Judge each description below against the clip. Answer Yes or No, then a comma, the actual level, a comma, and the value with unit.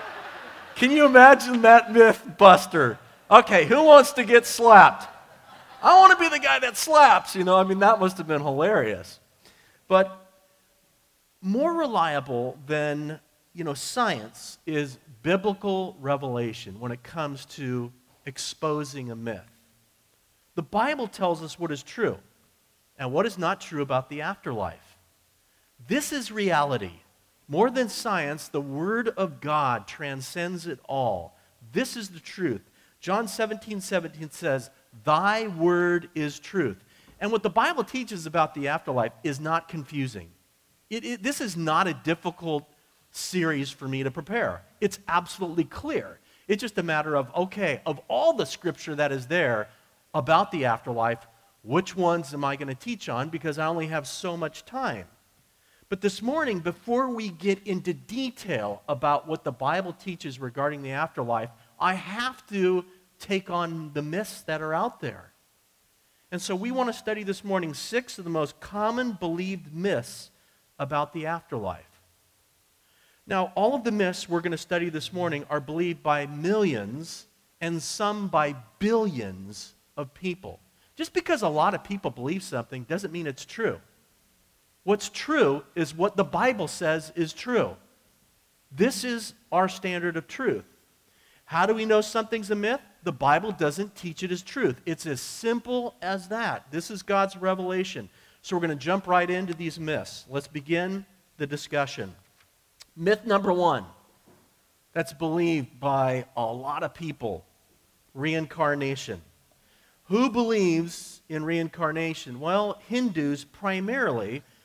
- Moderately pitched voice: Yes, medium, 170 Hz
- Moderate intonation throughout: No, wide, 5.7 semitones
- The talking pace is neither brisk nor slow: Yes, average, 150 wpm